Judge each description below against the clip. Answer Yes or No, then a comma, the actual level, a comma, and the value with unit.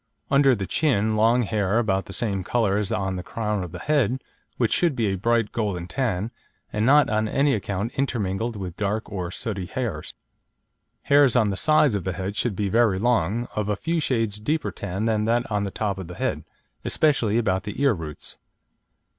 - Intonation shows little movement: No, average, 3.7 semitones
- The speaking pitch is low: Yes, low, 105 Hz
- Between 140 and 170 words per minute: No, average, 200 wpm